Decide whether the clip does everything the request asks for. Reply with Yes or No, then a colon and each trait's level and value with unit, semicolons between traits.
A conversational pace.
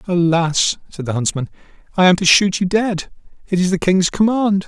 Yes: average, 195 wpm